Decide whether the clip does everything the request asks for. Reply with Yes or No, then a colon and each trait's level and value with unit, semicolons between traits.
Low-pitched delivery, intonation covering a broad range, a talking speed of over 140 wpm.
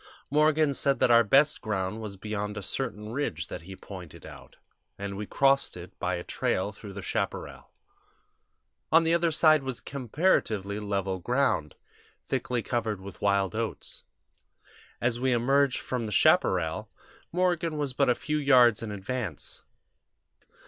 Yes: low, 115 Hz; wide, 5.7 semitones; average, 150 wpm